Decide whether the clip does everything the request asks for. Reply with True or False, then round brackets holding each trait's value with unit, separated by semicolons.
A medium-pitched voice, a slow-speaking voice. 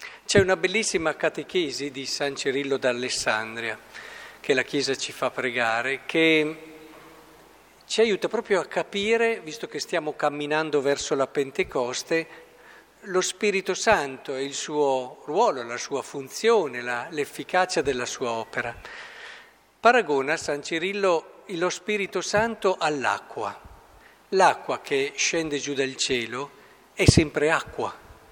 False (155 Hz; 125 wpm)